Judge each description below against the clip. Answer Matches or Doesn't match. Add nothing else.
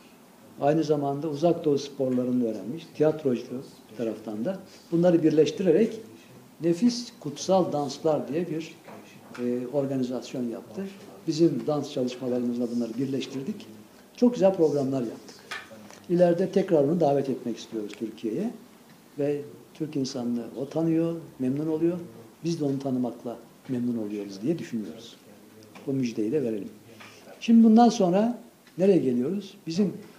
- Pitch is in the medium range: Matches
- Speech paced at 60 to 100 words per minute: Doesn't match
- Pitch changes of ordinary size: Doesn't match